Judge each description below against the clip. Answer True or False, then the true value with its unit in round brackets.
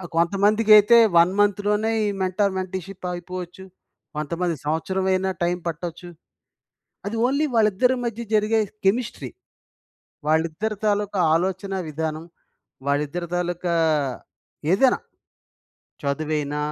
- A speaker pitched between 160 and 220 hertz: True (185 Hz)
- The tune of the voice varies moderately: True (3.6 semitones)